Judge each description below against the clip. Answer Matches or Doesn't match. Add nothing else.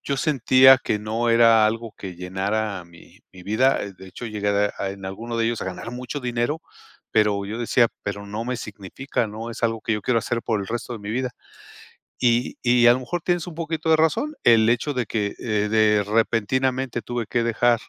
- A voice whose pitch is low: Matches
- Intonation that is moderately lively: Matches